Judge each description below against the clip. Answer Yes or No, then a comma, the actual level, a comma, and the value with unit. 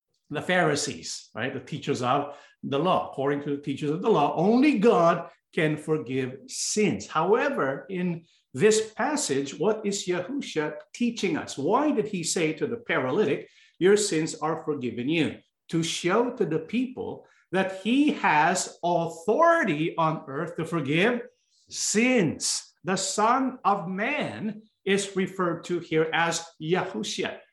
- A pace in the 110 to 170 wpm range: Yes, average, 140 wpm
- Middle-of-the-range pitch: Yes, medium, 175 Hz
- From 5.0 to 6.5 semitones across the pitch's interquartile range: Yes, wide, 5.6 semitones